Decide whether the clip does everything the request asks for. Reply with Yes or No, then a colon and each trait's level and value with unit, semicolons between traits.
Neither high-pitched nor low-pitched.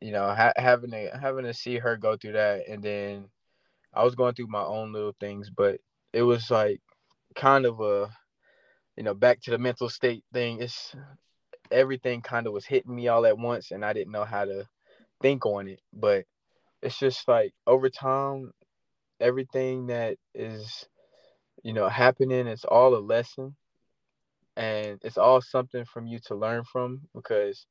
No: low, 120 Hz